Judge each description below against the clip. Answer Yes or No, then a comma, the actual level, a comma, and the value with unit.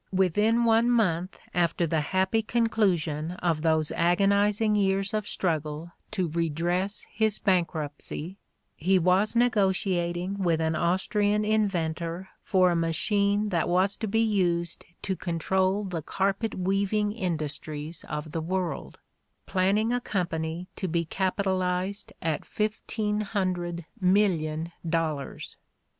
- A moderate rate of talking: No, slow, 125 wpm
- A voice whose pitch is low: No, medium, 185 Hz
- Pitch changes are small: No, average, 3.5 semitones